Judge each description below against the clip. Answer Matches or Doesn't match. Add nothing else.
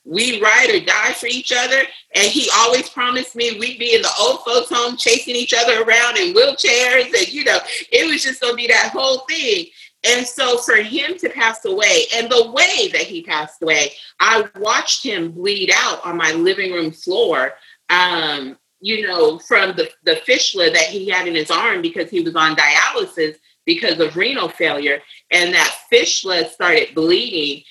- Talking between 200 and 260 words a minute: Doesn't match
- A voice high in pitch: Matches